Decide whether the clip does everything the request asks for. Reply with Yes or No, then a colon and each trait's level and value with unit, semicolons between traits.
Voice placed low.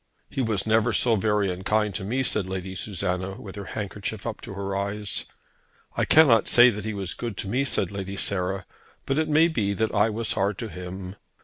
Yes: low, 100 Hz